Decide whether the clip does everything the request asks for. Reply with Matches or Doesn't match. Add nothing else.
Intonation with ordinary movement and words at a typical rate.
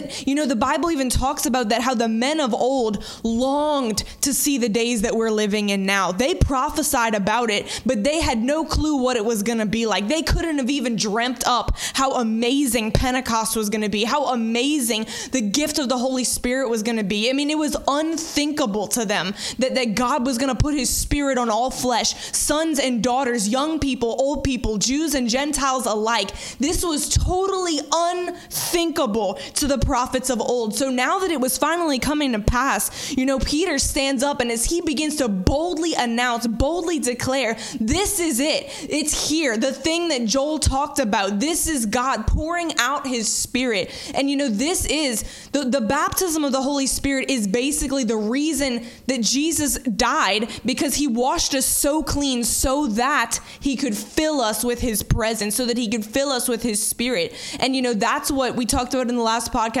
Matches